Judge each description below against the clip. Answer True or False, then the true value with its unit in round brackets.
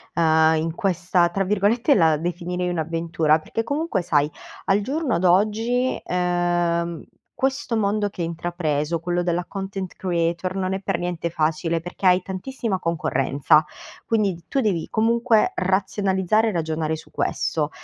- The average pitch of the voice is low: False (180 Hz)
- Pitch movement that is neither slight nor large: True (3.4 semitones)